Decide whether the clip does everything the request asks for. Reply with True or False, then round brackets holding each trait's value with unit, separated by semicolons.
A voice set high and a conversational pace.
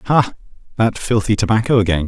False (110 Hz; 145 wpm)